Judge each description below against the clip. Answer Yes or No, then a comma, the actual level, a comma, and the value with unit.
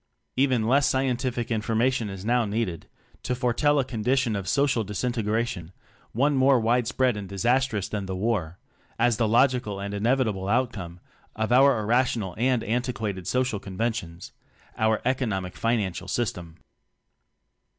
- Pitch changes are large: No, average, 3.8 semitones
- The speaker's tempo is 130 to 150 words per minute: Yes, average, 140 wpm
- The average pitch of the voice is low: Yes, low, 115 Hz